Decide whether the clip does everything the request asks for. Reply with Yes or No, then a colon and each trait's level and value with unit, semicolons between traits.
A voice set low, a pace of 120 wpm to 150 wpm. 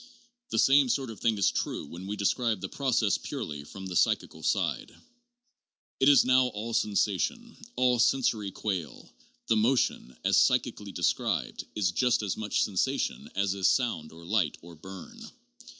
No: low, 105 Hz; average, 165 wpm